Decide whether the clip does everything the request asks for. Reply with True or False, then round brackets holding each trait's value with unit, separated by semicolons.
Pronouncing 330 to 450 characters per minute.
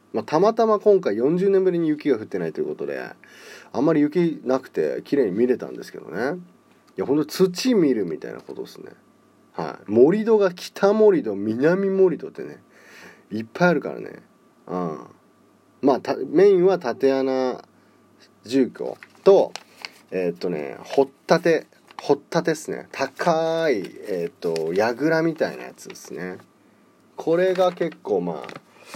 False (295 characters per minute)